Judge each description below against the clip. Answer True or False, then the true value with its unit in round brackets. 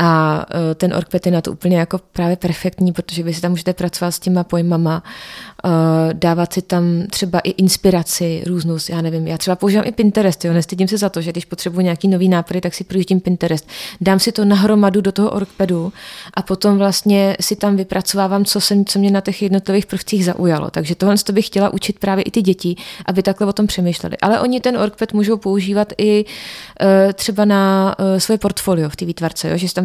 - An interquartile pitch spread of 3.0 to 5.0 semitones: False (2.4 semitones)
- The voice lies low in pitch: False (190 Hz)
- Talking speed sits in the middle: False (205 wpm)